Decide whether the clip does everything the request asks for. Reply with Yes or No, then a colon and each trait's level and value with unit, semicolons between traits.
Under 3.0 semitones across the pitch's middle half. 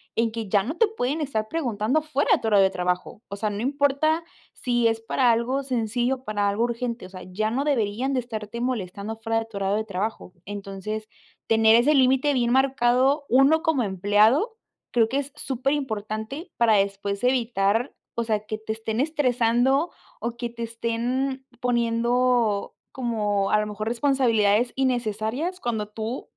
No: average, 3.6 semitones